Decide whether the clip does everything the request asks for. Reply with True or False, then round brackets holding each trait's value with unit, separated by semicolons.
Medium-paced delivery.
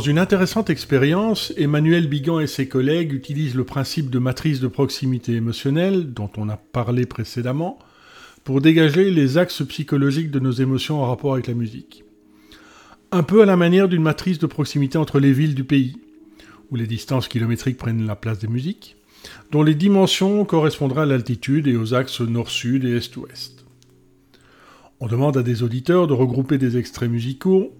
True (170 wpm)